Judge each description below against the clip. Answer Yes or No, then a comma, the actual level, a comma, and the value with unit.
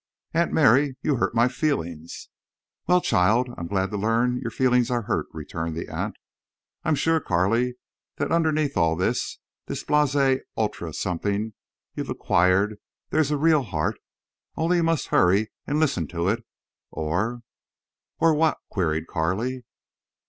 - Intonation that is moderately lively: No, wide, 8.1 semitones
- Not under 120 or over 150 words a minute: Yes, average, 140 wpm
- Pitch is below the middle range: Yes, low, 115 Hz